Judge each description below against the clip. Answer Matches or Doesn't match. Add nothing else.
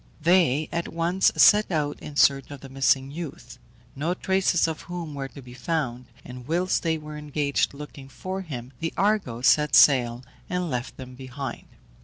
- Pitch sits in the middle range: Matches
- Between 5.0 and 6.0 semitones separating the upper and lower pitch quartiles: Doesn't match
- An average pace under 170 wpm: Doesn't match